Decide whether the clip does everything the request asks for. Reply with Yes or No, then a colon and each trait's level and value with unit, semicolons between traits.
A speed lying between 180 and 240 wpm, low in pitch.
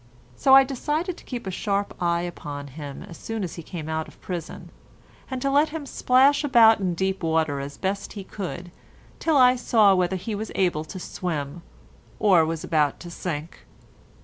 No: average, 190 wpm; medium, 185 Hz